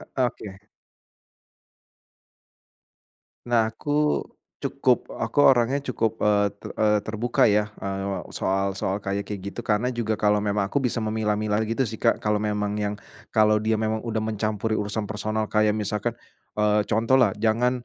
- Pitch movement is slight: Yes, narrow, 1.4 semitones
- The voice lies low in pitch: Yes, low, 110 Hz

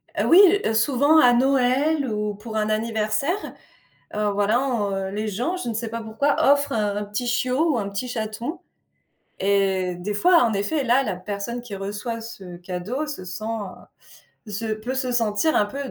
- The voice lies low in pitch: No, high, 225 Hz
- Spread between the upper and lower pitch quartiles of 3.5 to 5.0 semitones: Yes, average, 4.3 semitones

